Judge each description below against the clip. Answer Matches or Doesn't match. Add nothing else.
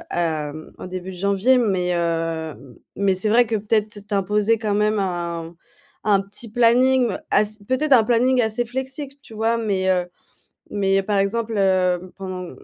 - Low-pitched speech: Doesn't match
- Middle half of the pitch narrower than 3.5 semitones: Doesn't match